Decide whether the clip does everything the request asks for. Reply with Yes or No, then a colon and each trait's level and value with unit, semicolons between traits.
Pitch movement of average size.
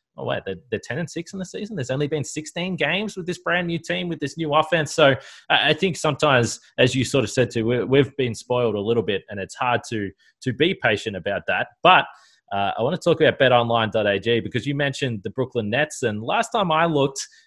No: wide, 5.9 semitones